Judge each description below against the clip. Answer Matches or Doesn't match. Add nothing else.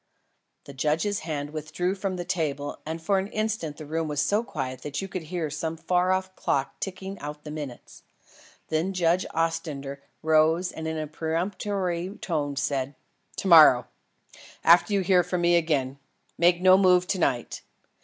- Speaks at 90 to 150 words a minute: Doesn't match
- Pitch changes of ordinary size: Matches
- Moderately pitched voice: Matches